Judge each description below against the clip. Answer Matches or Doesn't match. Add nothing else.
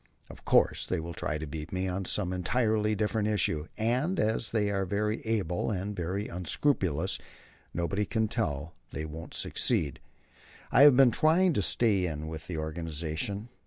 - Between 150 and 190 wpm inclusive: Matches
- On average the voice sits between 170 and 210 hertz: Doesn't match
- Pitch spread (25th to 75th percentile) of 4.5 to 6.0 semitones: Matches